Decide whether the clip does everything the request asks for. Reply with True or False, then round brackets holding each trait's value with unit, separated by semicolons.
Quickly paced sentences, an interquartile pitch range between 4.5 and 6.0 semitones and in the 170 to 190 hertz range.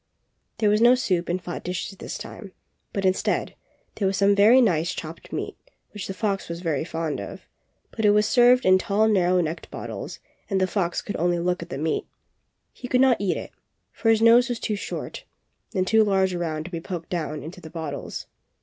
False (215 wpm; 3.7 semitones; 185 Hz)